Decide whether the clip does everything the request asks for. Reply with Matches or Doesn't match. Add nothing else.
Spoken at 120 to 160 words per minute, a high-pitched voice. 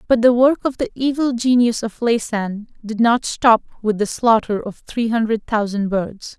Doesn't match